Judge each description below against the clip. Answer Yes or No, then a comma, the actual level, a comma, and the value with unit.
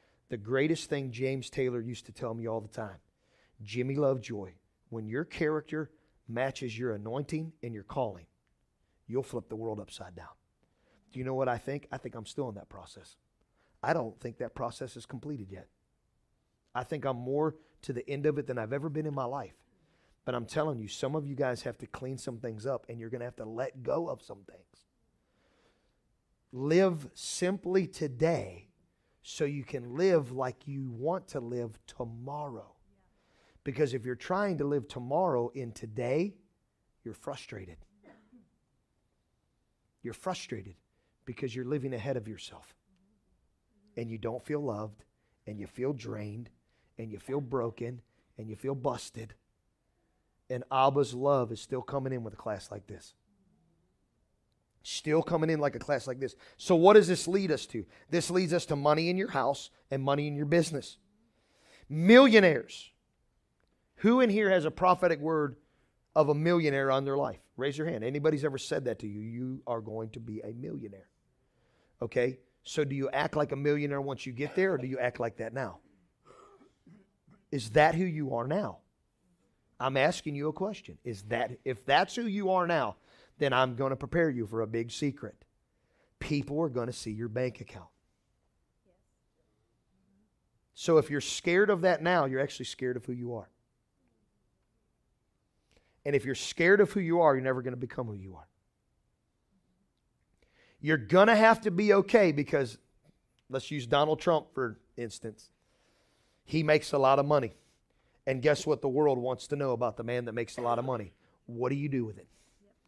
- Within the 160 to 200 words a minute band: Yes, average, 180 wpm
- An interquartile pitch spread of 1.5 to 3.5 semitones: No, average, 4.7 semitones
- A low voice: Yes, low, 130 Hz